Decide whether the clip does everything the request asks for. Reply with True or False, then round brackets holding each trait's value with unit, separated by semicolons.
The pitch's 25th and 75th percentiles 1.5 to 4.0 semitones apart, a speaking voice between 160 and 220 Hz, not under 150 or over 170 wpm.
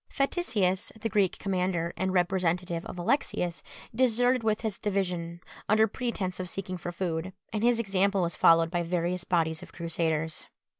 True (3.5 semitones; 185 Hz; 155 wpm)